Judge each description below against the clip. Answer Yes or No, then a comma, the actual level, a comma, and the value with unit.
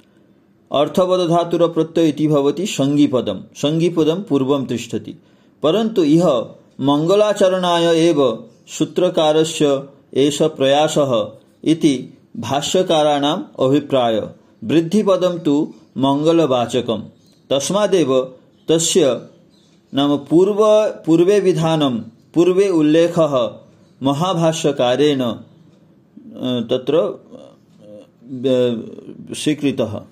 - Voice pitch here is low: No, medium, 155 Hz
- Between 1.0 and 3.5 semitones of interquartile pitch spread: No, average, 4.0 semitones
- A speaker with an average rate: No, slow, 70 wpm